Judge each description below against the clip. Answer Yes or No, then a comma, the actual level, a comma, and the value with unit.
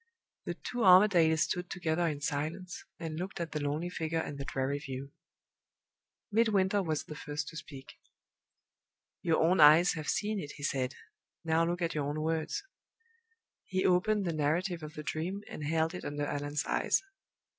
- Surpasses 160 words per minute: Yes, average, 170 wpm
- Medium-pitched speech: Yes, medium, 160 Hz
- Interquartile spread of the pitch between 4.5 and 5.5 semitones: No, average, 3.5 semitones